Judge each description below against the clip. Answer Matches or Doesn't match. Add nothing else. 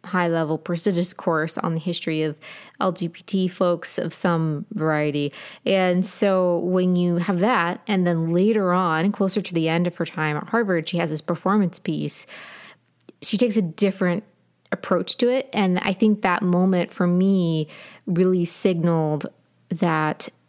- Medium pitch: Matches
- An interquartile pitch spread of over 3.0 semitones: Doesn't match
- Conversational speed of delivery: Matches